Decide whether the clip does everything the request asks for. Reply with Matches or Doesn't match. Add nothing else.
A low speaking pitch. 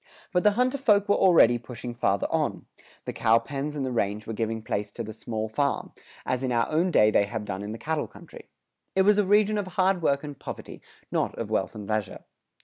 Matches